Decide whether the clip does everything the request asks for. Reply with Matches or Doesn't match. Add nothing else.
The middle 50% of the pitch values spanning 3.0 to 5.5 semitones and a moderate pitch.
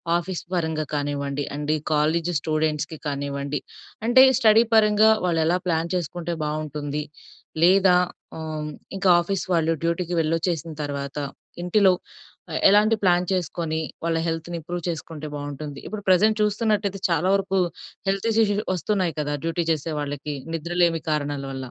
Matches